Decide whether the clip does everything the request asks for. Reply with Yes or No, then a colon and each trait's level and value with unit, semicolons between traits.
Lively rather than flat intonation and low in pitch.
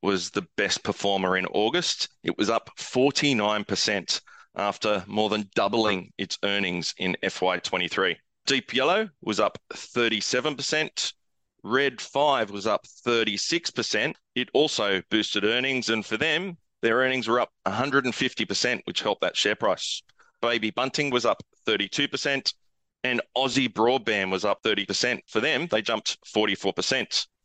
No: average, 4.4 semitones; low, 110 Hz